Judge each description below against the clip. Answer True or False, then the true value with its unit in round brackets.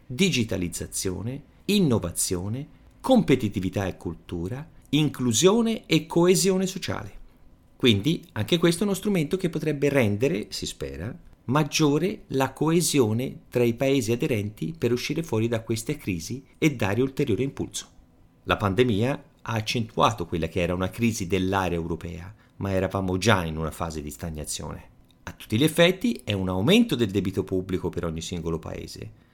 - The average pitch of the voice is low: True (115 Hz)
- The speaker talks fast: False (145 wpm)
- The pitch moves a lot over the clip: True (8.0 semitones)